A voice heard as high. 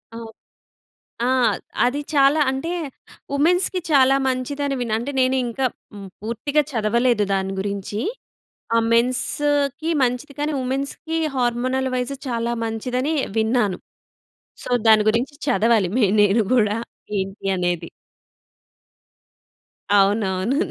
Yes: high, 245 Hz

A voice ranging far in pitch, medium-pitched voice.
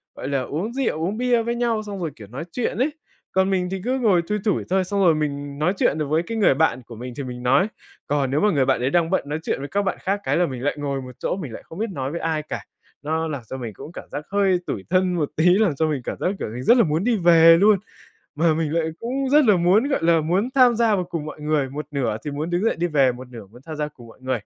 Yes: wide, 5.8 semitones; medium, 165 Hz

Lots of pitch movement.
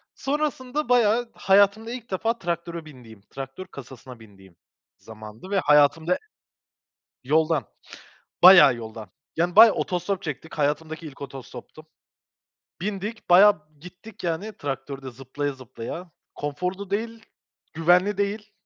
Yes: wide, 7.0 semitones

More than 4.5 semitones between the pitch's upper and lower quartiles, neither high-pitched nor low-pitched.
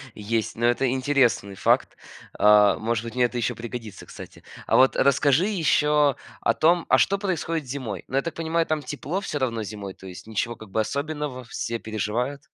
No: average, 5.1 semitones; low, 125 Hz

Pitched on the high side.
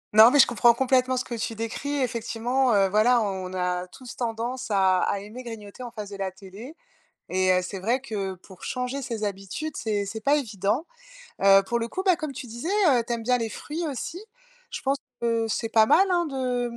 Yes: high, 230 Hz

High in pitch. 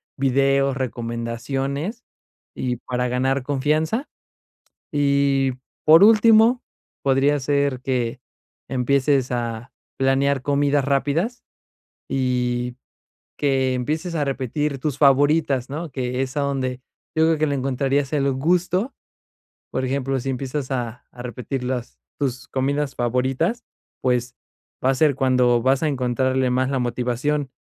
No: low, 135 Hz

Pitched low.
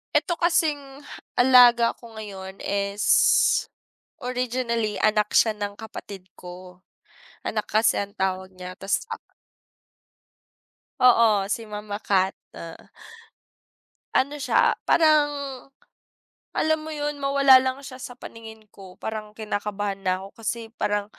No: high, 220 Hz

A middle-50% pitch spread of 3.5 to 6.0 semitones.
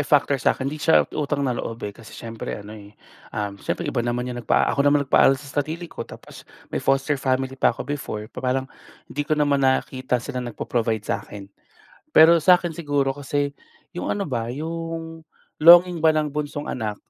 Yes: average, 4.0 semitones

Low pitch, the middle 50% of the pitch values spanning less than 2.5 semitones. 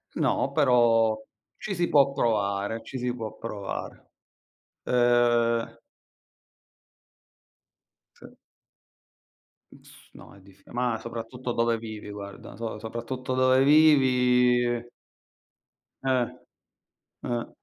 Yes: low, 120 Hz; narrow, 2.1 semitones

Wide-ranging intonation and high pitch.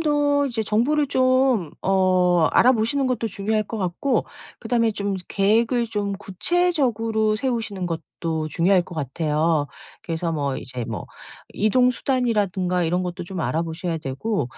Yes: wide, 5.9 semitones; high, 200 Hz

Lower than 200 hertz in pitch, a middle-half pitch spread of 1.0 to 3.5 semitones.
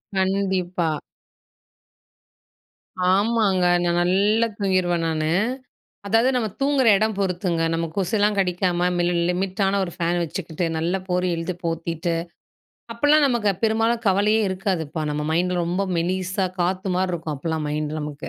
Yes: medium, 185 Hz; average, 2.9 semitones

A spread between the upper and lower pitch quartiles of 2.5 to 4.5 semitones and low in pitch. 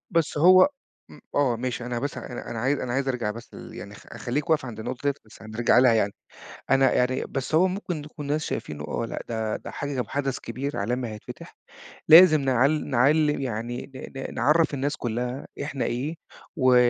Yes: average, 3.5 semitones; low, 130 Hz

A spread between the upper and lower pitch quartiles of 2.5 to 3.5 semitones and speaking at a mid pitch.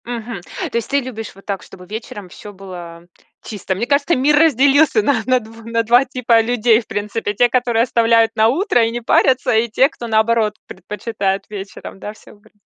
No: average, 3.0 semitones; high, 230 Hz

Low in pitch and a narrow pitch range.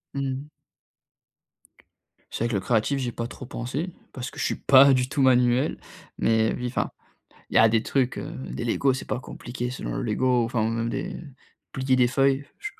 Yes: low, 125 Hz; narrow, 2.3 semitones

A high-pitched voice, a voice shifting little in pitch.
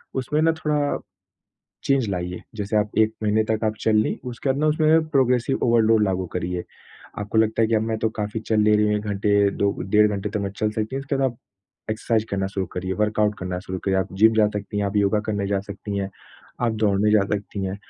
No: low, 105 Hz; narrow, 2.1 semitones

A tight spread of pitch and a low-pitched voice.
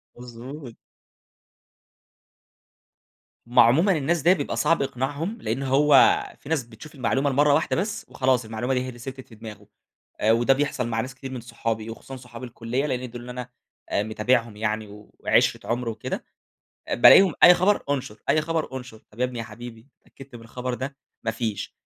No: average, 3.4 semitones; low, 125 Hz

